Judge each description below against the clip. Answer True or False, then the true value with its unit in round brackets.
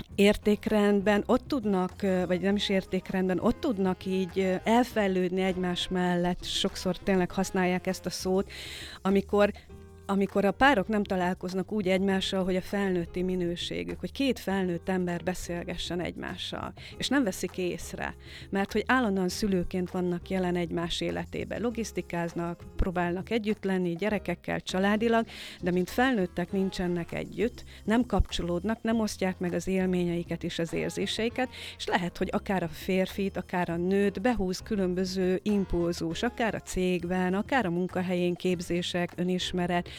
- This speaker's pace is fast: False (135 wpm)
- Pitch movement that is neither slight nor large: False (2.2 semitones)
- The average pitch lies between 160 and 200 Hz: True (185 Hz)